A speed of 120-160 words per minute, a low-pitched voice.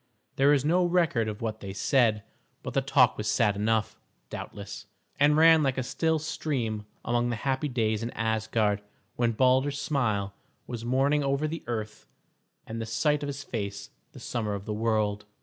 No: average, 180 wpm; low, 120 Hz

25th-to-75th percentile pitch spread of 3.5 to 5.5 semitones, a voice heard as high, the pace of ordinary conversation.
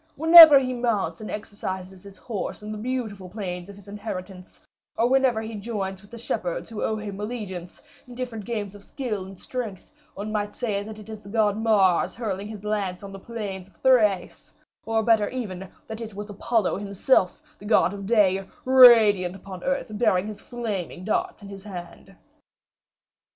No: average, 2.8 semitones; high, 210 Hz; average, 180 wpm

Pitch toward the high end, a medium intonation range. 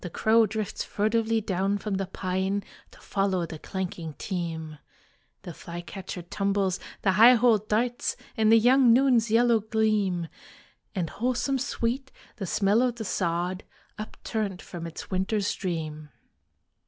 Yes: high, 200 Hz; average, 3.9 semitones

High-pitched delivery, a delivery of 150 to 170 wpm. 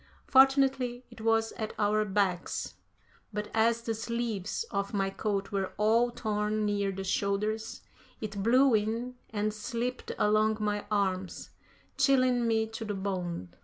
No: high, 215 Hz; average, 140 wpm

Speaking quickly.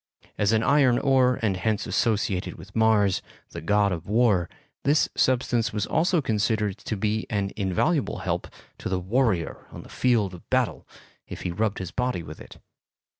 No: average, 175 wpm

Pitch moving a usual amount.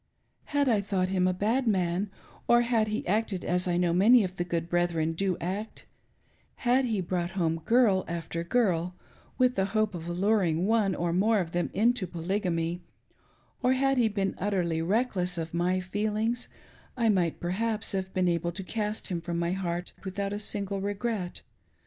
Yes: average, 3.7 semitones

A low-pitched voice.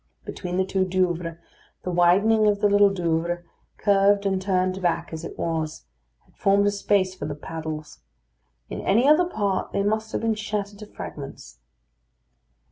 No: high, 190 Hz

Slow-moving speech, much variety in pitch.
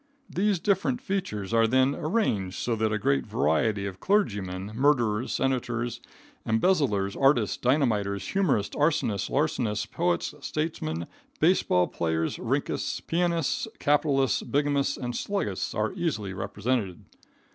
Yes: slow, 120 wpm; wide, 7.1 semitones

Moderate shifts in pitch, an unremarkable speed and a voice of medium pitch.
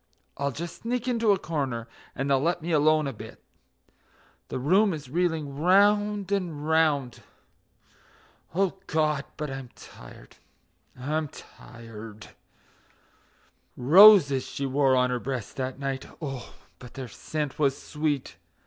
No: average, 4.5 semitones; slow, 130 wpm; medium, 145 Hz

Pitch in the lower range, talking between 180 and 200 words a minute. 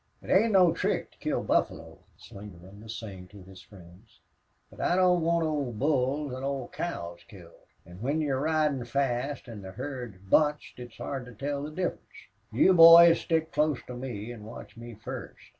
Yes: low, 130 Hz; average, 190 wpm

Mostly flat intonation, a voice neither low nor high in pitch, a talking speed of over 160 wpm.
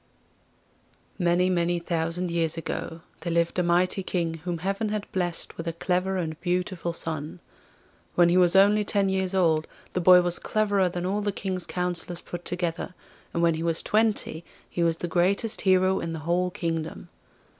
Yes: narrow, 1.9 semitones; medium, 175 Hz; average, 175 wpm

